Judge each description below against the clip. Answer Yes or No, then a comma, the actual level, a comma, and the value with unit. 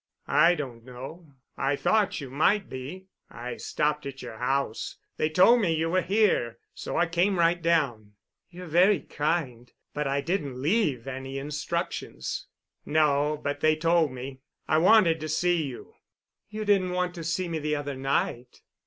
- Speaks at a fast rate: No, average, 160 wpm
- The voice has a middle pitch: Yes, medium, 155 Hz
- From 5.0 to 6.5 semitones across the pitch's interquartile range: No, average, 4.4 semitones